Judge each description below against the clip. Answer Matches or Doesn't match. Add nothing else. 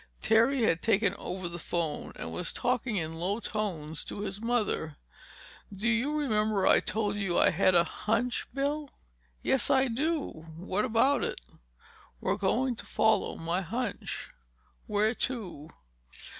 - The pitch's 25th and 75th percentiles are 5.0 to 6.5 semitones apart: Matches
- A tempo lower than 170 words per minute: Matches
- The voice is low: Doesn't match